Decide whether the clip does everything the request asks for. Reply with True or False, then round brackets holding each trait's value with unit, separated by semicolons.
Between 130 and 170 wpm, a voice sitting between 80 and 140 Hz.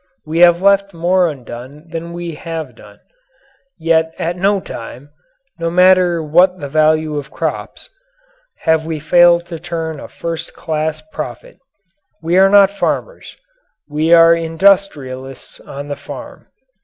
False (140 wpm; 165 Hz)